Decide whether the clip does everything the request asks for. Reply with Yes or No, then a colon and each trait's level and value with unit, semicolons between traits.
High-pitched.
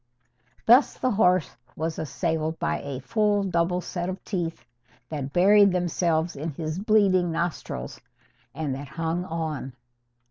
No: medium, 170 Hz